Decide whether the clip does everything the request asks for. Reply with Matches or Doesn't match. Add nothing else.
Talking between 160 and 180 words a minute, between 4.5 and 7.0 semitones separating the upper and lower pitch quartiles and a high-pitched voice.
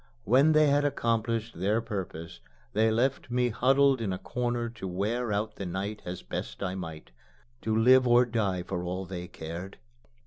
Doesn't match